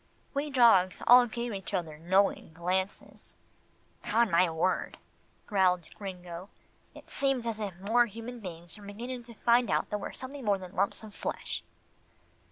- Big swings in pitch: No, average, 4.4 semitones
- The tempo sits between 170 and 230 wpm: No, average, 160 wpm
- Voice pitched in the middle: No, high, 205 Hz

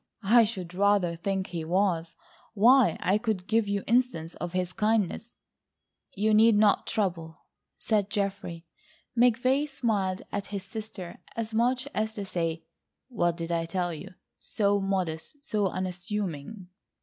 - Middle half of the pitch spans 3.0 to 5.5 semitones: Yes, average, 3.6 semitones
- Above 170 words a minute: No, average, 140 wpm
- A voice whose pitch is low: No, high, 200 Hz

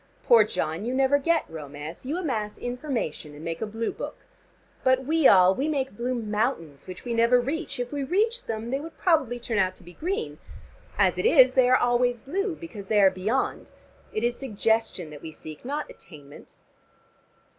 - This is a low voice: No, high, 240 Hz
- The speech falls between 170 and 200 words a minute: Yes, average, 190 wpm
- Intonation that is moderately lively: No, wide, 5.8 semitones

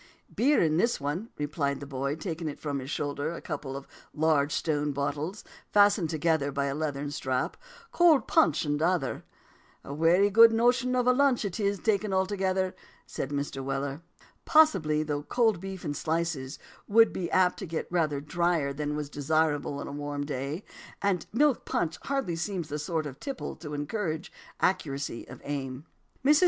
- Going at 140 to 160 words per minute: No, average, 175 wpm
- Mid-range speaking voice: Yes, medium, 160 Hz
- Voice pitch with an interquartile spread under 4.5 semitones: No, average, 5.1 semitones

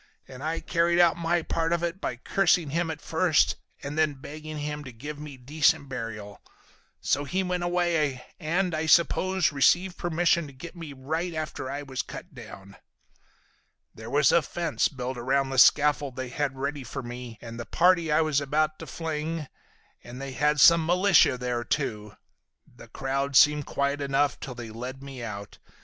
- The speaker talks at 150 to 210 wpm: Yes, average, 180 wpm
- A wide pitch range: No, average, 4.0 semitones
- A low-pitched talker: No, medium, 145 Hz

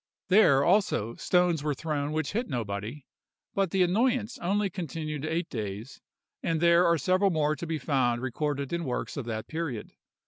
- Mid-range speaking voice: Yes, medium, 155 Hz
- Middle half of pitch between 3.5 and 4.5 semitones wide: No, average, 4.9 semitones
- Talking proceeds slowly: No, average, 170 wpm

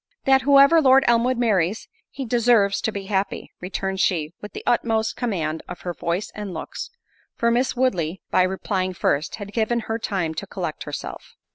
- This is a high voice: Yes, high, 210 Hz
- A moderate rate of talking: Yes, average, 175 wpm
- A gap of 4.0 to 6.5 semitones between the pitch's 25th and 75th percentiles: Yes, average, 4.5 semitones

